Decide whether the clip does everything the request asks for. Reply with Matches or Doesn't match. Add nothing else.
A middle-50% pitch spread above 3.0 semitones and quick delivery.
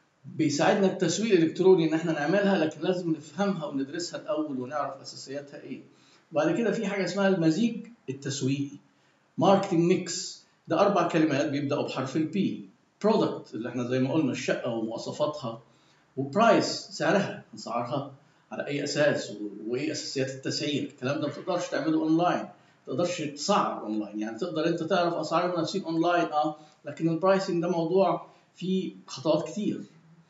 Matches